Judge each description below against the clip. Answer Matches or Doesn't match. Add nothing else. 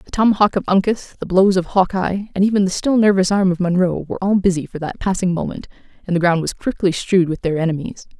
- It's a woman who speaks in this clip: Matches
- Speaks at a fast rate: Matches